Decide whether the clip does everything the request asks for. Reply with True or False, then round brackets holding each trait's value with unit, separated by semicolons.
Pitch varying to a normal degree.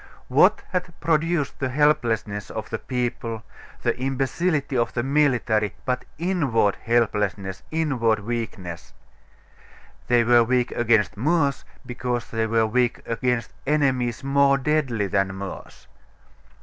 True (3.9 semitones)